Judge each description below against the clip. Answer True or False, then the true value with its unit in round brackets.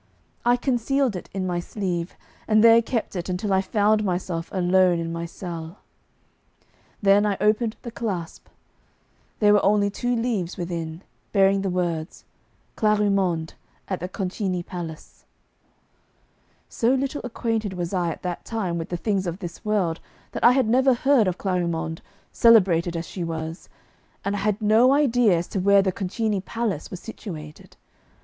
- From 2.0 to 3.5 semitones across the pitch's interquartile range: False (4.0 semitones)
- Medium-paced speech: True (160 wpm)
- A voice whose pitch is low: False (195 Hz)